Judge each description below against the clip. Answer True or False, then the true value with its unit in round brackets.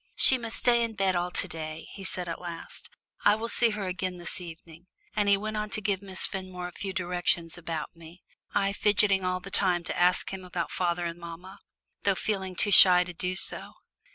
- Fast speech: True (215 wpm)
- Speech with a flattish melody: True (2.3 semitones)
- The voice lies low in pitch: False (185 Hz)